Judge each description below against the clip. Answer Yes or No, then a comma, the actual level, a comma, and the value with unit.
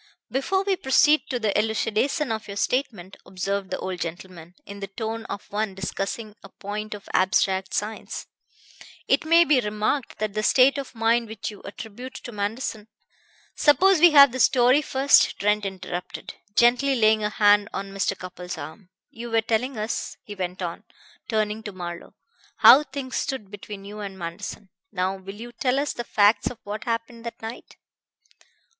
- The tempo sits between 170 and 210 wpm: Yes, average, 175 wpm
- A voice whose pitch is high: Yes, high, 215 Hz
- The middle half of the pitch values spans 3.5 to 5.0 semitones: Yes, average, 3.9 semitones